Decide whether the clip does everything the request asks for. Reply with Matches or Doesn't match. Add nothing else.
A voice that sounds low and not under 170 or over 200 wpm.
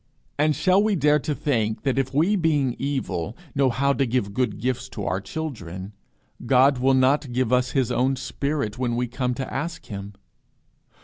Matches